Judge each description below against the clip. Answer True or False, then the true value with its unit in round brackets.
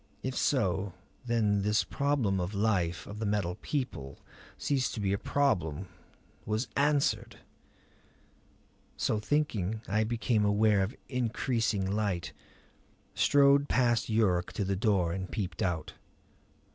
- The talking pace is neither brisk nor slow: False (130 wpm)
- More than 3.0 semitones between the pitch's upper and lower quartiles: True (4.0 semitones)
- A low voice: True (105 Hz)